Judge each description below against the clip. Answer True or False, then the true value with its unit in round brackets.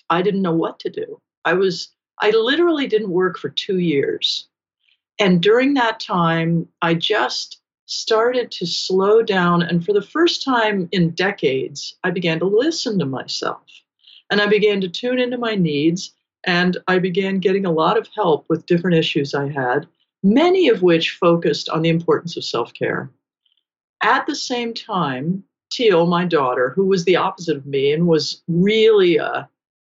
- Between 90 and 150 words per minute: False (170 wpm)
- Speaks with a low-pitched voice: False (190 Hz)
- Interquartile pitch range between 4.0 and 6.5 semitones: True (5.0 semitones)